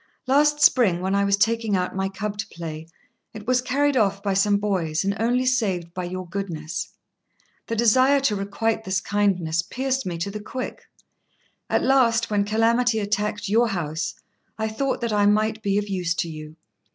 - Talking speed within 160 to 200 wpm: Yes, average, 185 wpm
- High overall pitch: Yes, high, 205 Hz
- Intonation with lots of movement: No, average, 3.7 semitones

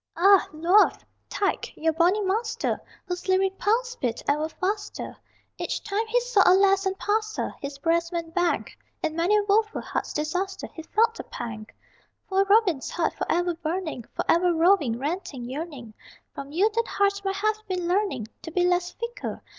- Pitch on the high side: Yes, very high, 365 Hz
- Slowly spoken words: No, average, 170 wpm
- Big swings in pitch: No, average, 3.9 semitones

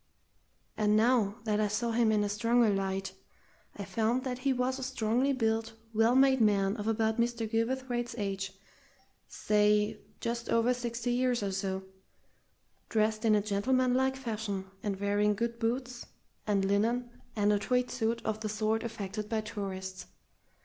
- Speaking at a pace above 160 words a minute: No, average, 155 wpm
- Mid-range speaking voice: No, high, 220 Hz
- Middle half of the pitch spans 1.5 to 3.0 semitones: Yes, narrow, 2.6 semitones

